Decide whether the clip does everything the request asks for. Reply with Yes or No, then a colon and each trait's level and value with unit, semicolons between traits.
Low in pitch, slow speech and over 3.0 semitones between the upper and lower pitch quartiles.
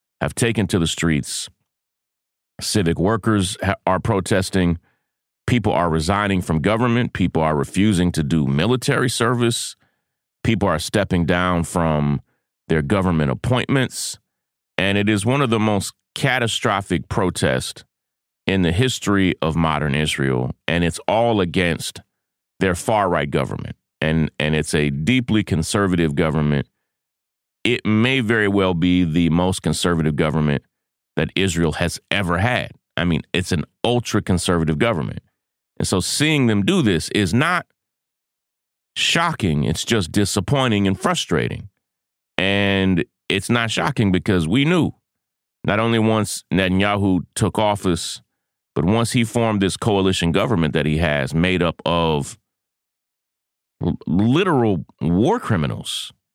Yes: very low, 95 Hz; slow, 130 wpm; average, 5.0 semitones